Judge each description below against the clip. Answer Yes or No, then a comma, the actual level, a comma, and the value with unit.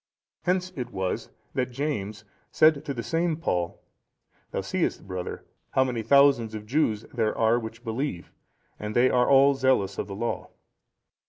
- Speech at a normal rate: Yes, average, 160 wpm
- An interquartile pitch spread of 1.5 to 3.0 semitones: No, average, 4.6 semitones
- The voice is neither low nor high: No, low, 120 Hz